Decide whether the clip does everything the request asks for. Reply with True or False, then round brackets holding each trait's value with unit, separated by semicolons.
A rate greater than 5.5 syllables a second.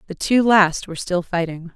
False (5.1 syllables/s)